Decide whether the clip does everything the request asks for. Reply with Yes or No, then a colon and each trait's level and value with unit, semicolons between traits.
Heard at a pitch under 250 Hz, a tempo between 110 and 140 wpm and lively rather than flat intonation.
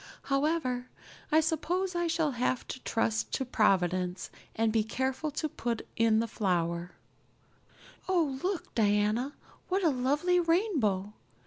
No: very high, 255 Hz; slow, 135 wpm; wide, 6.9 semitones